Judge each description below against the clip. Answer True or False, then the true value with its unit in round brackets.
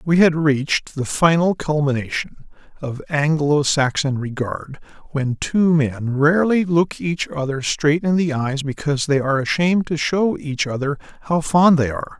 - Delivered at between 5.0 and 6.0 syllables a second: False (4.6 syllables/s)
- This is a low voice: False (150 Hz)